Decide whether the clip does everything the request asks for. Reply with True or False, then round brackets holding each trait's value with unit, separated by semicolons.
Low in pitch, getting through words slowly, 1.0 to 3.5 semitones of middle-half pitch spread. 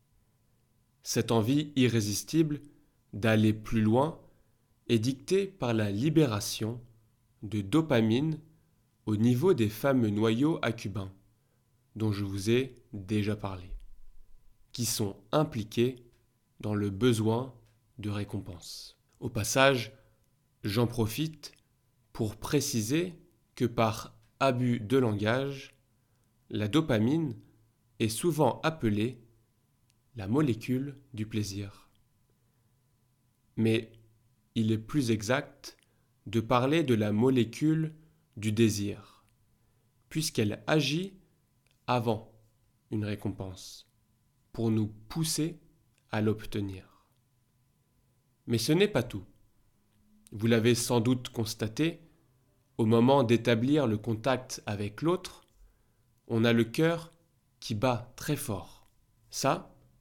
True (115 Hz; 100 wpm; 2.9 semitones)